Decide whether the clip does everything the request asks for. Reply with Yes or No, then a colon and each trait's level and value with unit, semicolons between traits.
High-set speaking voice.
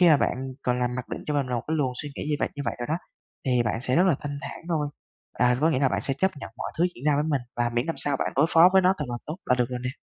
No: medium, 140 Hz